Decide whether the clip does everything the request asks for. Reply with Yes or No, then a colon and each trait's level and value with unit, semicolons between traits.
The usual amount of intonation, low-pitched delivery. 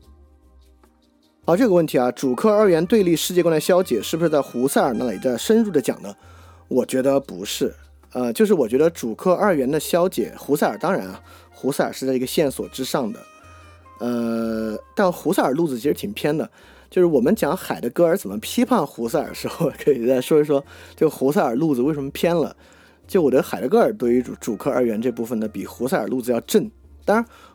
No: wide, 8.9 semitones; low, 130 Hz